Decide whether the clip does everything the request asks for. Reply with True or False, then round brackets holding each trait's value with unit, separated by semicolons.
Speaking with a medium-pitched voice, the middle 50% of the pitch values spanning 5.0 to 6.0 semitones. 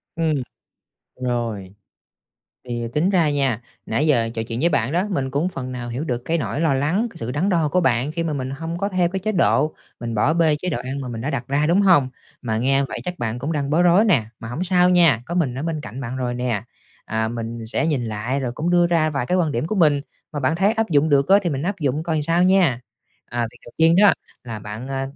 True (145 Hz; 5.6 semitones)